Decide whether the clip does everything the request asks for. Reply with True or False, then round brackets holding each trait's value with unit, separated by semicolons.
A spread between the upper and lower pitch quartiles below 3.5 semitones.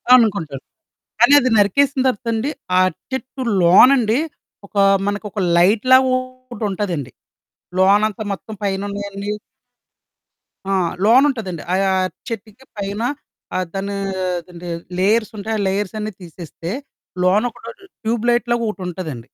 False (3.8 semitones)